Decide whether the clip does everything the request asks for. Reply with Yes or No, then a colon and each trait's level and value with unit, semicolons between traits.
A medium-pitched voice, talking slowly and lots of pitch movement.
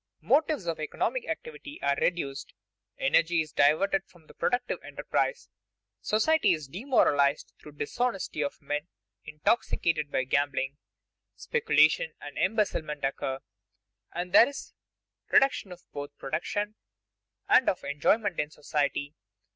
Yes: medium, 165 Hz; slow, 120 wpm; wide, 8.4 semitones